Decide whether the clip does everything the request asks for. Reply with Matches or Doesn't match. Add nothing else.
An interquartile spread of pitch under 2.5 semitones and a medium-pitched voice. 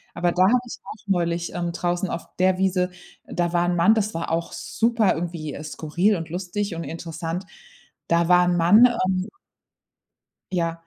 Matches